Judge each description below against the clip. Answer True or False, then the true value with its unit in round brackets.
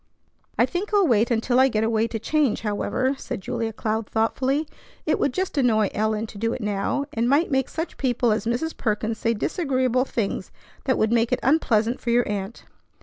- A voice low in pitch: False (235 Hz)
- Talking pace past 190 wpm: True (200 wpm)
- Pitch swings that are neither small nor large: True (3.4 semitones)